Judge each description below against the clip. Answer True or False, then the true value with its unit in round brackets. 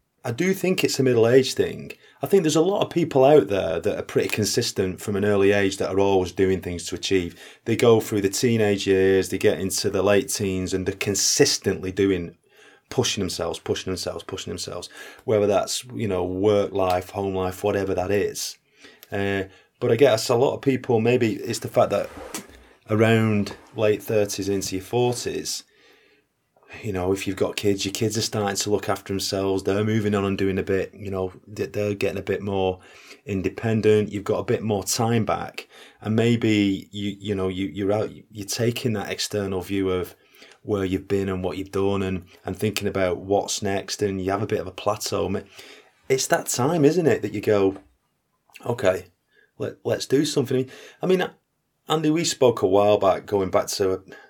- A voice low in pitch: True (100 Hz)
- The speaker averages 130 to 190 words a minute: False (200 wpm)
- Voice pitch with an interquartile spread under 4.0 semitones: True (2.7 semitones)